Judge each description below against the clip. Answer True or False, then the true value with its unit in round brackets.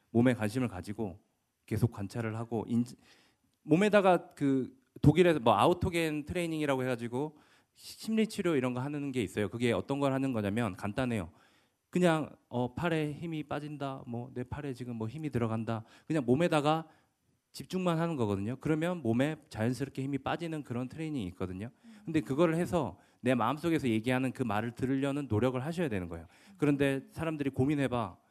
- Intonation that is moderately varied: True (4.8 semitones)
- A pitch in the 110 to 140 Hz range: True (135 Hz)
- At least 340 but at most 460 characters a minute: True (380 characters per minute)